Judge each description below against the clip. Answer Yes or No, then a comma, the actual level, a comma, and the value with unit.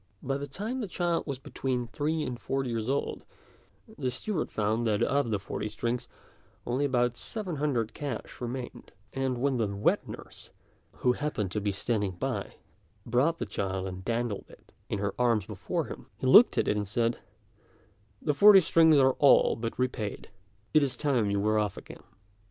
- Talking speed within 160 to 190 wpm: Yes, average, 180 wpm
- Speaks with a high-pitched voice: No, low, 125 Hz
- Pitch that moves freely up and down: No, average, 4.8 semitones